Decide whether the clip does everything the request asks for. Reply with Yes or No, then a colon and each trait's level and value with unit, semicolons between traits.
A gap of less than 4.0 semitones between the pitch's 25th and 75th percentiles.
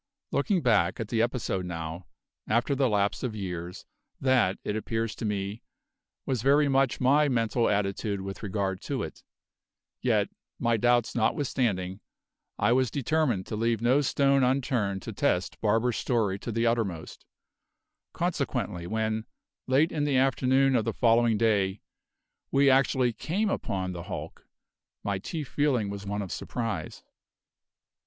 No: average, 4.6 semitones